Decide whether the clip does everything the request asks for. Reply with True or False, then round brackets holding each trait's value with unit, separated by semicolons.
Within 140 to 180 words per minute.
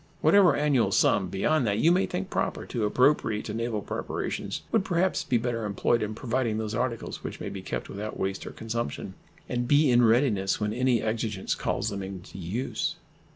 False (190 wpm)